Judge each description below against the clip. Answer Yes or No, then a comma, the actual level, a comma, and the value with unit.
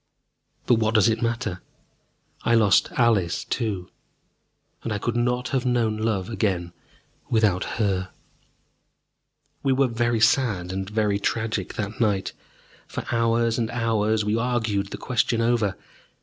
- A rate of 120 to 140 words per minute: Yes, slow, 135 wpm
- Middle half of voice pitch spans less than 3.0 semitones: Yes, narrow, 2.5 semitones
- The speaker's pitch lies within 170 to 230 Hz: No, low, 110 Hz